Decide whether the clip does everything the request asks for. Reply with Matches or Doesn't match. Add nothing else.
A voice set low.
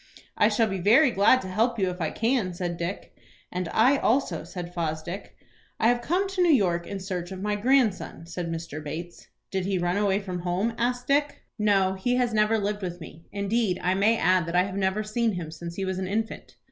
Doesn't match